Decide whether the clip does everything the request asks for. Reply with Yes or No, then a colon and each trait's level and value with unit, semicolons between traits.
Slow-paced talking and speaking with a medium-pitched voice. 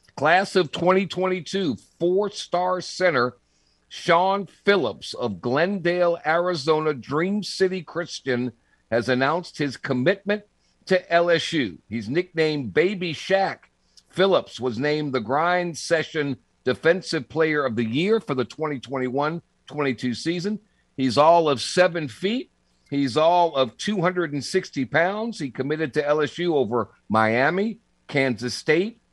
Yes: slow, 120 wpm; medium, 160 Hz